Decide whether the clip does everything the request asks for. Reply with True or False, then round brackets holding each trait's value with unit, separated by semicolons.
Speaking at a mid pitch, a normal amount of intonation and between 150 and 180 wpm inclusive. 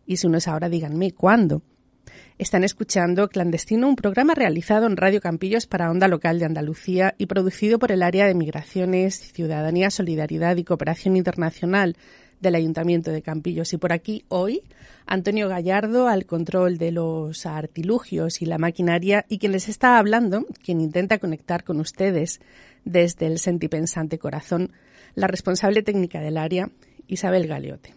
True (180 Hz; 3.1 semitones; 155 wpm)